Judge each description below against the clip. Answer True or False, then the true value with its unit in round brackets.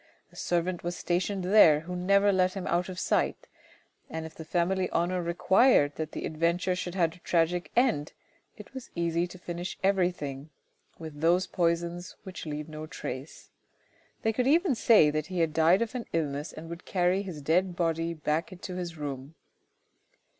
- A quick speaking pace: False (175 wpm)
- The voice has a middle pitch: True (175 Hz)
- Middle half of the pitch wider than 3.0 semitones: False (2.5 semitones)